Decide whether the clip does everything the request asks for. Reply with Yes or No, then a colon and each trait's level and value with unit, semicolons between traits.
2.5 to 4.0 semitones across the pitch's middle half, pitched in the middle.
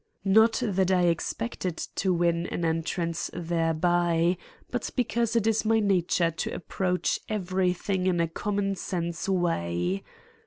Yes: average, 2.8 semitones; medium, 180 Hz